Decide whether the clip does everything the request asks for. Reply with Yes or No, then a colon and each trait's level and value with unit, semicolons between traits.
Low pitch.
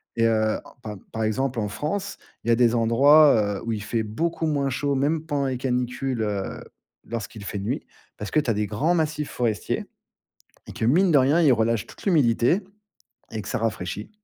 Yes: low, 120 Hz